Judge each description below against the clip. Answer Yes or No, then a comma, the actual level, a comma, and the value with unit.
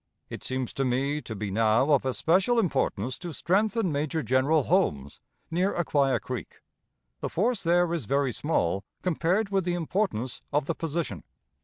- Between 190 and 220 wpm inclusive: No, average, 160 wpm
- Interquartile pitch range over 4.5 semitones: Yes, wide, 5.5 semitones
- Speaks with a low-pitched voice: No, medium, 150 Hz